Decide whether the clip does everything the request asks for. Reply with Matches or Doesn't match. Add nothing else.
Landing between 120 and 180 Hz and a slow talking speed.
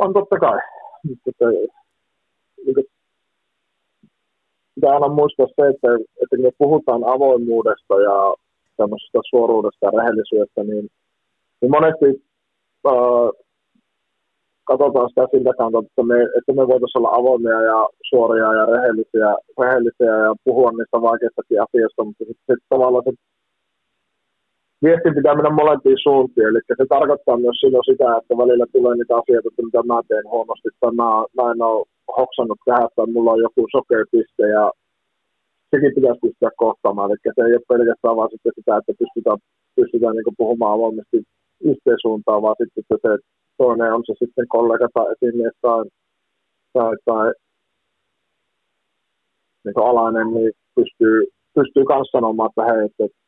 Doesn't match